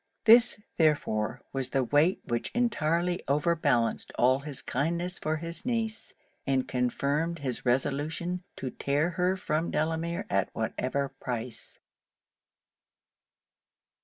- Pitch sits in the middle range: Yes, medium, 150 Hz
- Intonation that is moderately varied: Yes, average, 4.6 semitones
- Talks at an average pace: No, slow, 115 wpm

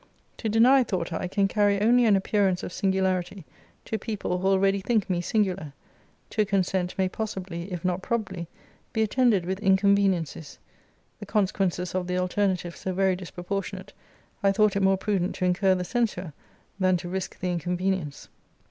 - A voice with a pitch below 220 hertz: Yes, high, 190 Hz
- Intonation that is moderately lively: No, narrow, 2.0 semitones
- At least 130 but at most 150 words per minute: No, average, 165 wpm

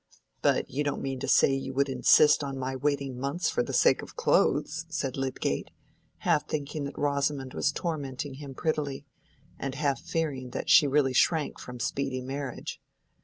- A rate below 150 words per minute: No, average, 170 wpm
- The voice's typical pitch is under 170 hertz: Yes, medium, 140 Hz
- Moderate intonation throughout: No, narrow, 1.9 semitones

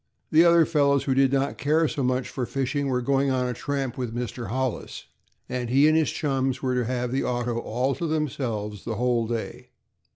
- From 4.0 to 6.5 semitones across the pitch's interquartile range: No, narrow, 2.4 semitones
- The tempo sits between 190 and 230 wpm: Yes, fast, 205 wpm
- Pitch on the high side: No, low, 130 Hz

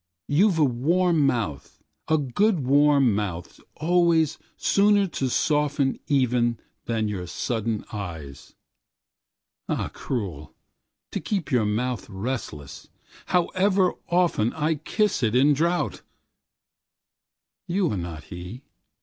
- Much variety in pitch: Yes, wide, 7.6 semitones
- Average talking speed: No, slow, 90 wpm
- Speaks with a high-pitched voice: No, low, 135 Hz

